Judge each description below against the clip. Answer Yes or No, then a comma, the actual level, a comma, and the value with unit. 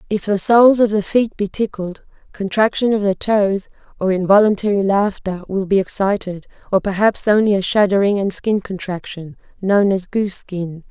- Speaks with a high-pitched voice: Yes, high, 200 Hz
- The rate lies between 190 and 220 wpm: No, average, 165 wpm